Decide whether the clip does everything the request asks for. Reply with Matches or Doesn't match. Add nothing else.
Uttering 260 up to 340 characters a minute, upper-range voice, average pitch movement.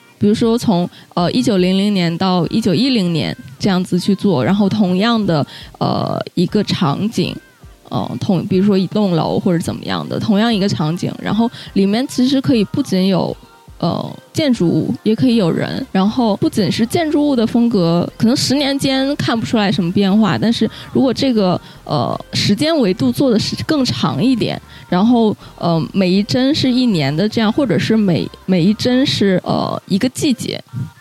Matches